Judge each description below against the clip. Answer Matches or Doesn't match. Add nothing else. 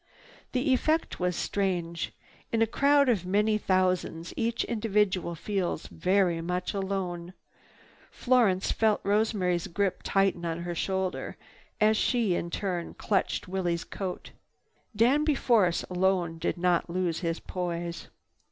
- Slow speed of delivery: Matches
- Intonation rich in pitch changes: Doesn't match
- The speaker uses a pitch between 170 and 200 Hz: Matches